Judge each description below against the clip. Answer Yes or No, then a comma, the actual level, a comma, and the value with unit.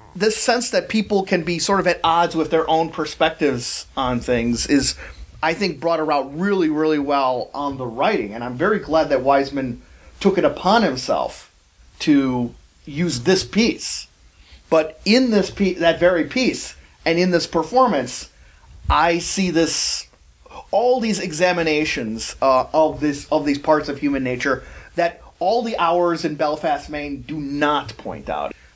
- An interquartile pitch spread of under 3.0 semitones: No, average, 4.3 semitones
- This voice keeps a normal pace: Yes, average, 165 wpm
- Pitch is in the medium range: Yes, medium, 155 Hz